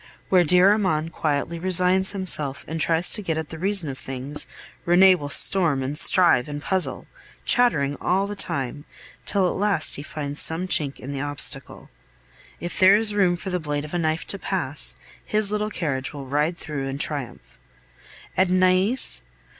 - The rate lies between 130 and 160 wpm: No, average, 180 wpm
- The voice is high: No, medium, 165 Hz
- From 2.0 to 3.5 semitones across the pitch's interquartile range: No, average, 4.5 semitones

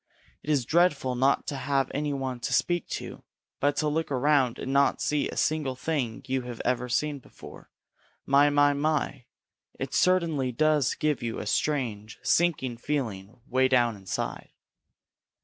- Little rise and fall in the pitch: No, average, 3.1 semitones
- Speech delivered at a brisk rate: No, average, 160 wpm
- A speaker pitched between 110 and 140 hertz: Yes, low, 135 Hz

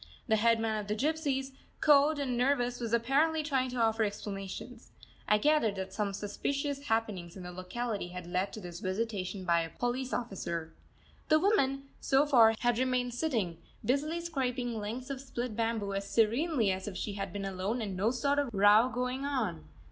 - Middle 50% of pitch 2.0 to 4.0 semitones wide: No, average, 5.0 semitones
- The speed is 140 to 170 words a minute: No, average, 180 wpm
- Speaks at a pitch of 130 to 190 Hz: No, high, 230 Hz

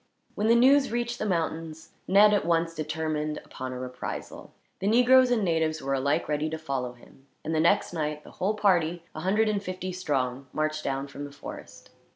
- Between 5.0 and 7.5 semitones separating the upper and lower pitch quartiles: Yes, average, 5.3 semitones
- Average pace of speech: Yes, average, 195 wpm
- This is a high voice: No, medium, 160 Hz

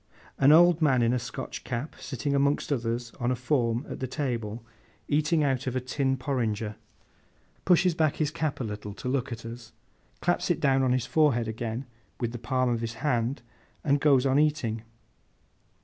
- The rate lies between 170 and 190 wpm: Yes, average, 185 wpm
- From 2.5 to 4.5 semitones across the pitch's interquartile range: Yes, average, 3.6 semitones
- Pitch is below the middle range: Yes, low, 130 Hz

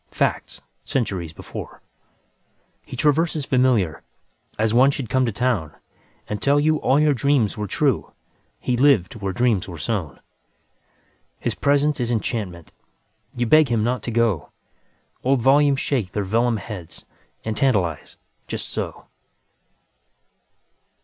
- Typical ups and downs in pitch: Yes, average, 4.8 semitones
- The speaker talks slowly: Yes, slow, 110 wpm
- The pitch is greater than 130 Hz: No, low, 120 Hz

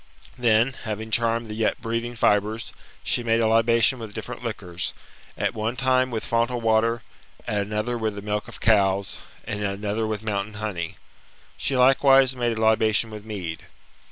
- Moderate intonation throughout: No, narrow, 2.0 semitones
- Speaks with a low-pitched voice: Yes, low, 110 Hz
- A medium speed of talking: Yes, average, 170 wpm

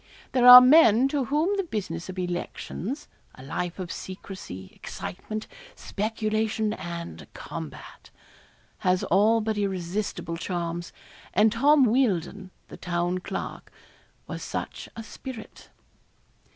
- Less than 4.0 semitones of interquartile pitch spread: No, average, 4.6 semitones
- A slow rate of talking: Yes, slow, 115 wpm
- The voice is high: Yes, high, 205 Hz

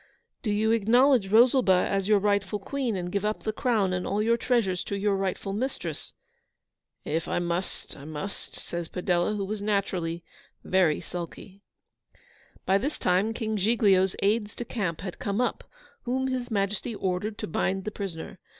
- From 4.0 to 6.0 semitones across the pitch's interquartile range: No, average, 3.0 semitones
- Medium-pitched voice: No, high, 200 Hz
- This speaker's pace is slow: No, average, 170 wpm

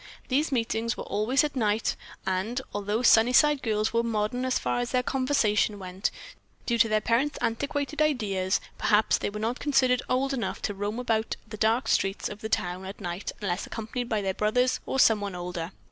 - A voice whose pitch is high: Yes, high, 225 Hz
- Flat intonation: No, average, 3.5 semitones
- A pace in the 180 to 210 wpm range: Yes, average, 190 wpm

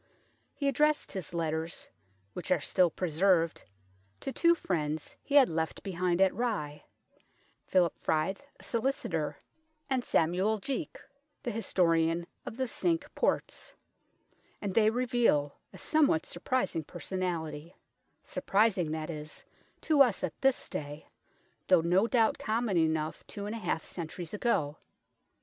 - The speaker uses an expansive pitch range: Yes, wide, 6.5 semitones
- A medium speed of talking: No, slow, 130 wpm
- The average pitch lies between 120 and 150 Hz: No, medium, 185 Hz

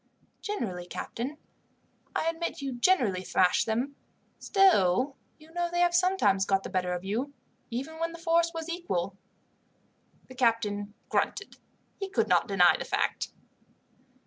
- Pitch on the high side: Yes, very high, 270 Hz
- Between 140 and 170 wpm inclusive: Yes, average, 145 wpm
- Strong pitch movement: Yes, wide, 8.9 semitones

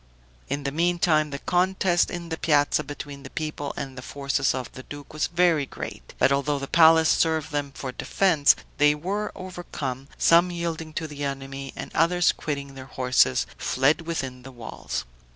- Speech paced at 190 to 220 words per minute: No, average, 175 wpm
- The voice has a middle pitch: Yes, medium, 150 Hz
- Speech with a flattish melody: No, average, 3.3 semitones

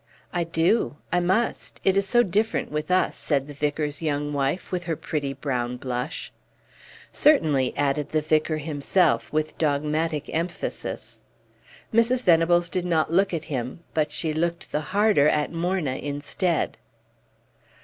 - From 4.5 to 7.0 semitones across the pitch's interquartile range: No, average, 3.4 semitones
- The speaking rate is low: No, average, 145 wpm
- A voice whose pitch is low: No, medium, 155 Hz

